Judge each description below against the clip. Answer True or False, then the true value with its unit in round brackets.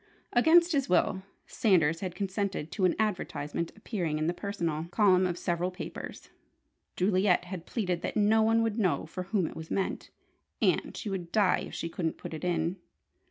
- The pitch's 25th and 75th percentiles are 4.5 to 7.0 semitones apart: False (3.5 semitones)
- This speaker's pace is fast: False (180 wpm)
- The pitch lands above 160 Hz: True (185 Hz)